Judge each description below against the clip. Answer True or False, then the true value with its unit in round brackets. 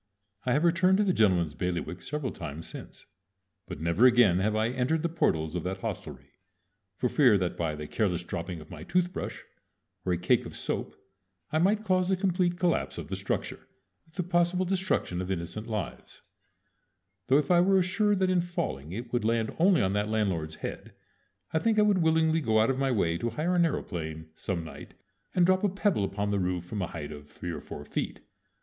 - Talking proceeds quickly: True (210 wpm)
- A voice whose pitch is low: True (115 Hz)